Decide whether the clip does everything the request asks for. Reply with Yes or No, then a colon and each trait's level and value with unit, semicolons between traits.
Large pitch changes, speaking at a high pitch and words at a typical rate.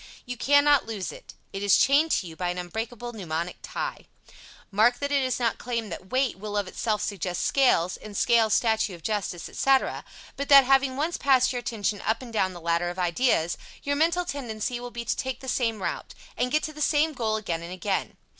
No: wide, 5.7 semitones; high, 230 Hz; fast, 215 wpm